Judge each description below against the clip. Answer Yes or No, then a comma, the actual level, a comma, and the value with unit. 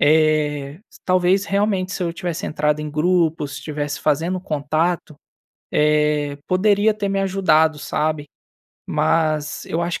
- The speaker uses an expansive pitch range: No, average, 3.5 semitones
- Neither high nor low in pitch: Yes, medium, 160 Hz